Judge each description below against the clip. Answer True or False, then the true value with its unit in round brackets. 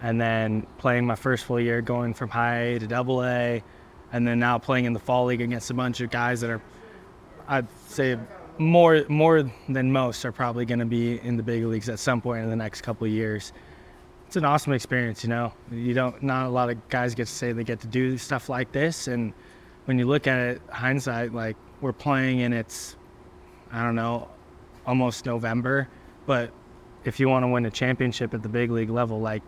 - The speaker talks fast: True (215 wpm)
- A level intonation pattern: True (1.6 semitones)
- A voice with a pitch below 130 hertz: True (120 Hz)